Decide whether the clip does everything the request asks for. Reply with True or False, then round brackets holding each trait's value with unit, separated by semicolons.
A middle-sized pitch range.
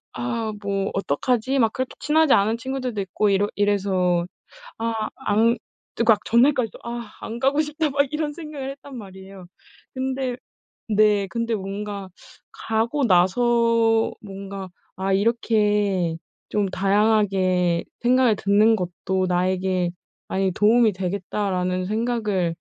True (3.8 semitones)